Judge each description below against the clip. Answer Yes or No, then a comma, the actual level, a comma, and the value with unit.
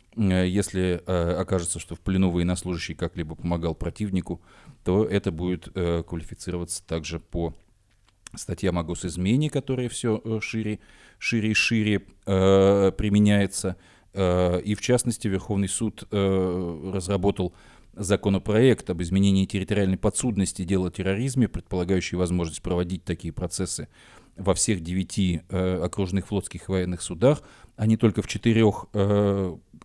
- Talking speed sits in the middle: Yes, average, 130 wpm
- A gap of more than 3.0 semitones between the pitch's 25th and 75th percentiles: No, average, 2.7 semitones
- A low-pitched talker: Yes, very low, 95 Hz